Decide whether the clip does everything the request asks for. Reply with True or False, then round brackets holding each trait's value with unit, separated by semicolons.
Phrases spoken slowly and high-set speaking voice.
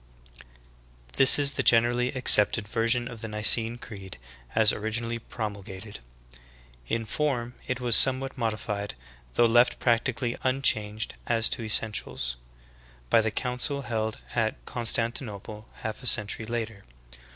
False (130 wpm; 115 Hz)